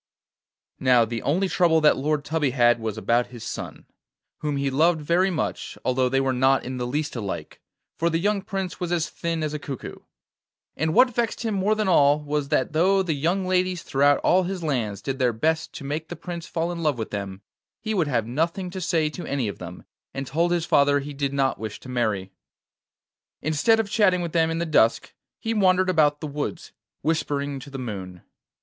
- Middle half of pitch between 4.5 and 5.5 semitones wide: Yes, average, 4.9 semitones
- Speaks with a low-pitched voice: No, medium, 150 Hz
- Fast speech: Yes, fast, 210 wpm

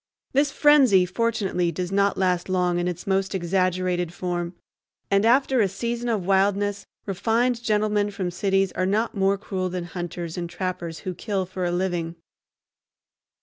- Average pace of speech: Yes, average, 155 wpm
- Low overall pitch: No, high, 190 Hz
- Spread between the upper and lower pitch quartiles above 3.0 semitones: No, narrow, 2.5 semitones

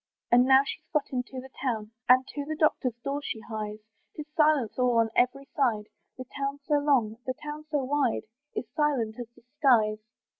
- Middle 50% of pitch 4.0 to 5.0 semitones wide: No, average, 3.6 semitones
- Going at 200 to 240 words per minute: No, average, 190 wpm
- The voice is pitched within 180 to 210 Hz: No, very high, 260 Hz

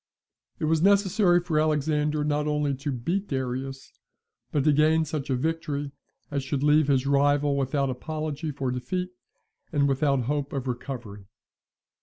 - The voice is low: No, medium, 145 Hz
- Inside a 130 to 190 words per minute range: Yes, average, 150 wpm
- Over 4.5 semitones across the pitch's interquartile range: No, narrow, 2.4 semitones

